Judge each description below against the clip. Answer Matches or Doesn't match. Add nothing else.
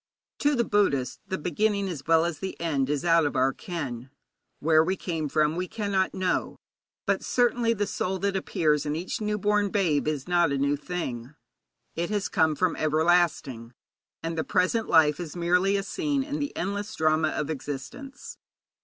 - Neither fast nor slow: Matches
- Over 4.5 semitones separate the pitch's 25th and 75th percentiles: Matches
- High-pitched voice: Doesn't match